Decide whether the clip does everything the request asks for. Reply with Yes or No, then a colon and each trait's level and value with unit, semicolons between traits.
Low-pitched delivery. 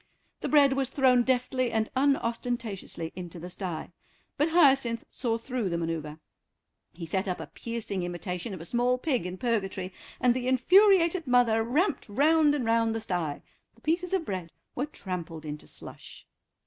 No: high, 235 Hz